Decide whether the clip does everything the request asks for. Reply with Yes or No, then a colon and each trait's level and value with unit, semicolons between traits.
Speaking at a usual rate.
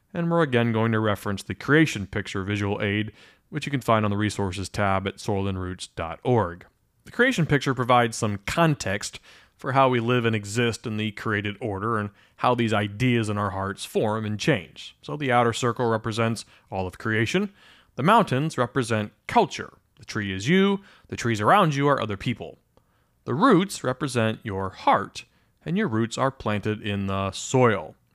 Yes: average, 175 wpm